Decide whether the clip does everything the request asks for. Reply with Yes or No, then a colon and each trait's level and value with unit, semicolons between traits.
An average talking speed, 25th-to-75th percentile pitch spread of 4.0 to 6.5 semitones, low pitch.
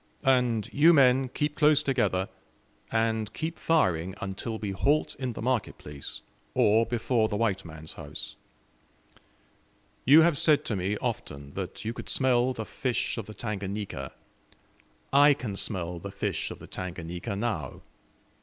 Yes: average, 150 wpm; average, 5.3 semitones; low, 110 Hz